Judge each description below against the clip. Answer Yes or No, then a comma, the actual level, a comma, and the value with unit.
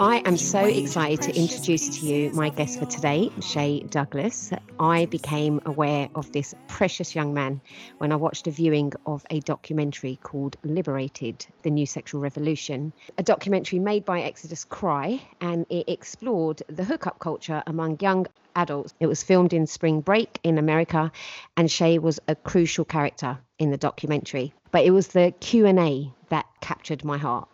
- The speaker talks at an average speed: Yes, average, 170 wpm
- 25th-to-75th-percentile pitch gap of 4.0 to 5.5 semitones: No, average, 3.1 semitones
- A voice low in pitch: No, medium, 155 Hz